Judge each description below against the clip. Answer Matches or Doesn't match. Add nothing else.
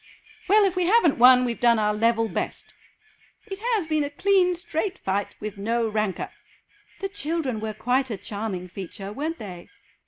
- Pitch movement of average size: Doesn't match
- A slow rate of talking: Doesn't match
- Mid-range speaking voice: Doesn't match